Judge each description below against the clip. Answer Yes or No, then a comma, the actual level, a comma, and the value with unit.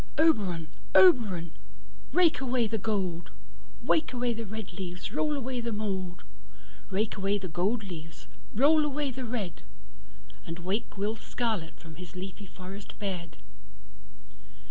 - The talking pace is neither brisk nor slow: No, slow, 120 wpm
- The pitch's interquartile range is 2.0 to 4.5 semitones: No, average, 5.1 semitones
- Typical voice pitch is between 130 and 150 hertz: No, high, 200 Hz